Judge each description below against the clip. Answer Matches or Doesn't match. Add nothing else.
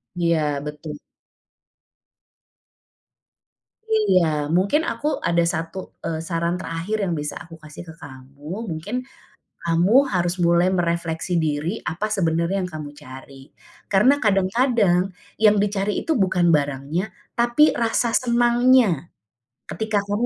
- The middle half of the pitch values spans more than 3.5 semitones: Matches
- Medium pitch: Matches